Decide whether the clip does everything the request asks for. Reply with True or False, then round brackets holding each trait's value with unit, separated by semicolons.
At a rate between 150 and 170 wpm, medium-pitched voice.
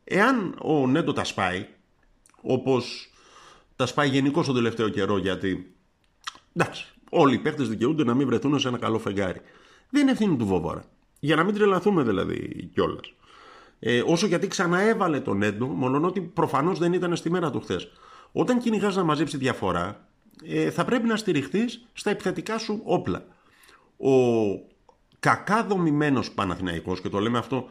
True (160 wpm; 145 Hz)